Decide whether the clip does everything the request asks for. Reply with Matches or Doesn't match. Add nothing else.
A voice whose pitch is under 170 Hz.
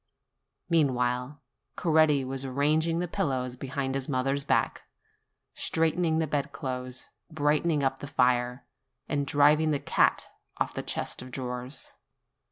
Matches